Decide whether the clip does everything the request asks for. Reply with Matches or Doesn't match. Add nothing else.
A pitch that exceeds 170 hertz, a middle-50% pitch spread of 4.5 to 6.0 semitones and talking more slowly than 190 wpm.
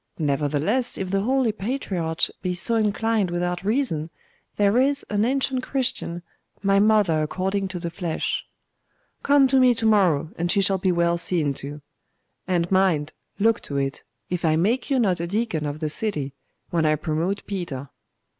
Matches